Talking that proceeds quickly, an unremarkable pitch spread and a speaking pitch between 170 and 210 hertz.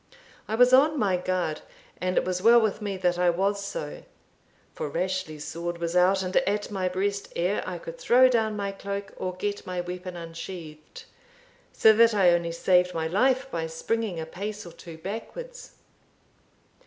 No: average, 180 wpm; average, 3.6 semitones; medium, 185 Hz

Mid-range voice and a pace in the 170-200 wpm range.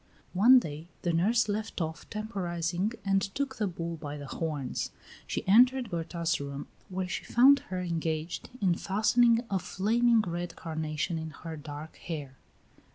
No: medium, 175 Hz; average, 155 wpm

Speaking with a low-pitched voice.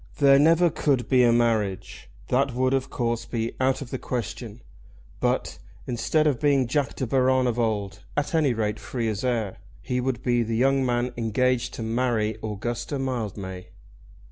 Yes: low, 120 Hz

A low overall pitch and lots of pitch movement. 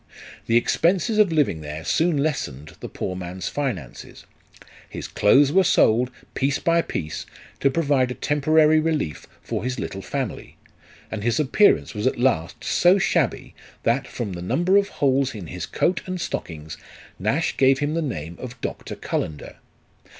Yes: low, 130 Hz; wide, 8.8 semitones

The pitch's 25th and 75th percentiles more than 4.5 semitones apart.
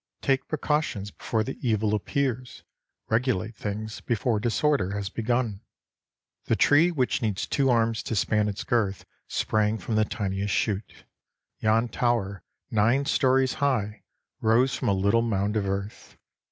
No: average, 3.5 semitones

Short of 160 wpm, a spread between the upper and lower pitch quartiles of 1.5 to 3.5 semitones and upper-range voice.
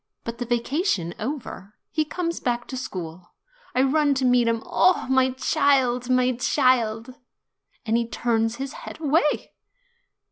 Yes: average, 150 wpm; average, 3.2 semitones; very high, 250 Hz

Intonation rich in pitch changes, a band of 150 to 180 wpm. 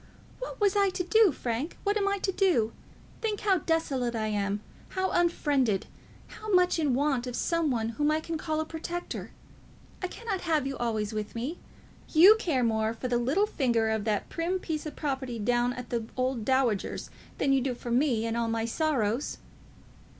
No: wide, 6.9 semitones; average, 195 wpm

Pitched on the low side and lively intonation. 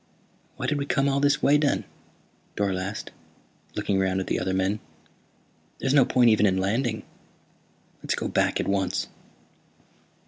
Yes: low, 105 Hz; wide, 6.3 semitones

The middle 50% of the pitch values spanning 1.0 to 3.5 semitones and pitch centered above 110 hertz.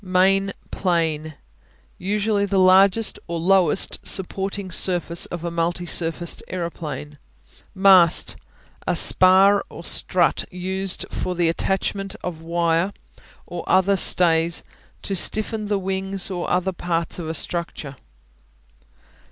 Yes: narrow, 2.4 semitones; medium, 185 Hz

